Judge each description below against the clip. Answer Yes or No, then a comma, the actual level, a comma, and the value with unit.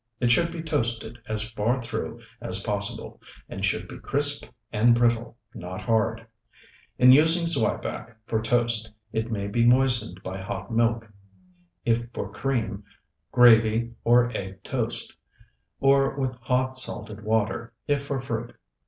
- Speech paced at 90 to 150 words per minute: Yes, average, 140 wpm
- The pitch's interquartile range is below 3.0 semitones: Yes, narrow, 2.6 semitones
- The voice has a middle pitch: No, low, 115 Hz